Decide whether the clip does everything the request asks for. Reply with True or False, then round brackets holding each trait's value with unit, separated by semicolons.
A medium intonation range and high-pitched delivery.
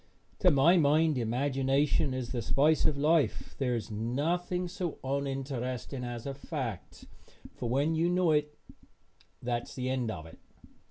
False (3.9 semitones; 135 Hz)